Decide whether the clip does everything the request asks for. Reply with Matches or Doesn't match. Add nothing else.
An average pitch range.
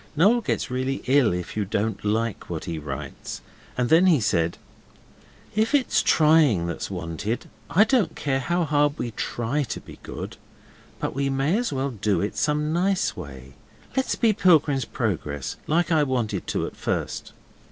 Doesn't match